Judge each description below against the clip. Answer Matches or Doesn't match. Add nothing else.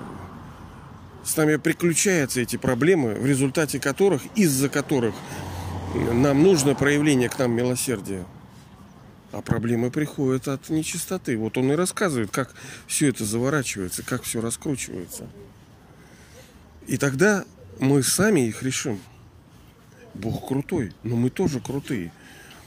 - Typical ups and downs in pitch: Matches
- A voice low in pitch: Matches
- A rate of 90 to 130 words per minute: Matches